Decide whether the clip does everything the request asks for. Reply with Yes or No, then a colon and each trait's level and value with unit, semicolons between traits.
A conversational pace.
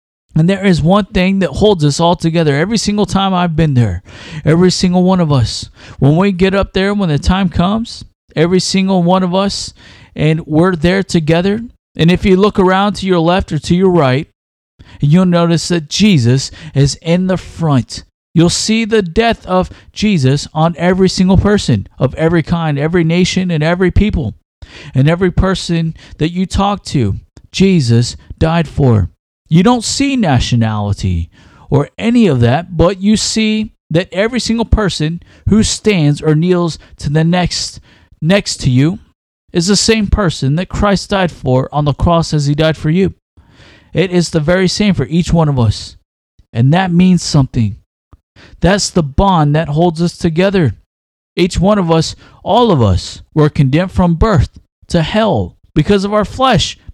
Yes: average, 175 wpm